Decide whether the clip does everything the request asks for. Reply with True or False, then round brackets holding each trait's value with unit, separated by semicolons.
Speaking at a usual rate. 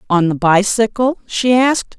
True (150 wpm)